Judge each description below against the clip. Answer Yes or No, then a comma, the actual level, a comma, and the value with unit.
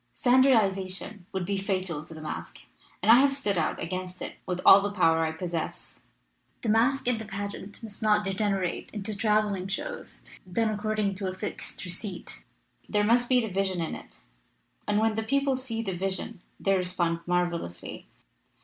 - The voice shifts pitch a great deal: No, average, 3.3 semitones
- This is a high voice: Yes, high, 200 Hz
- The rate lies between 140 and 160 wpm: No, average, 175 wpm